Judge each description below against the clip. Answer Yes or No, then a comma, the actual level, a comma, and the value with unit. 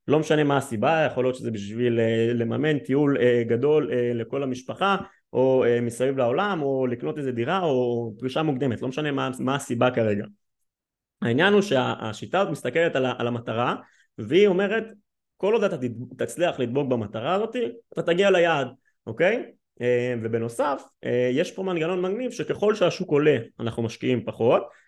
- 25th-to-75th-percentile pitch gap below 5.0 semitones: No, wide, 5.5 semitones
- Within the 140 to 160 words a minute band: Yes, average, 145 wpm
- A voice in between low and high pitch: No, low, 130 Hz